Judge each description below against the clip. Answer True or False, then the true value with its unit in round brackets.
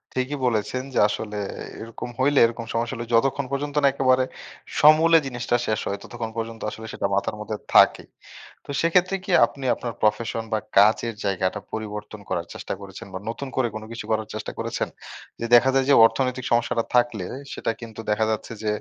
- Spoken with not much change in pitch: False (3.2 semitones)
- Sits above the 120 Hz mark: False (115 Hz)